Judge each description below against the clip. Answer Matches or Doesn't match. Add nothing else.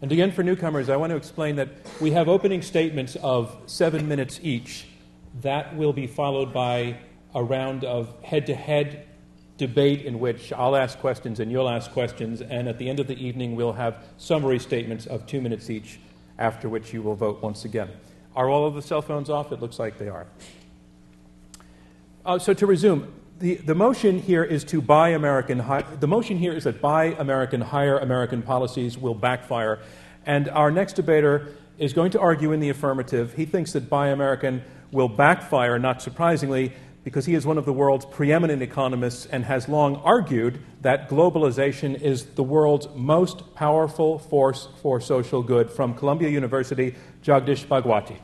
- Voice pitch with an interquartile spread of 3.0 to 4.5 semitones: Matches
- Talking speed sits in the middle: Matches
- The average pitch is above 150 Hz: Doesn't match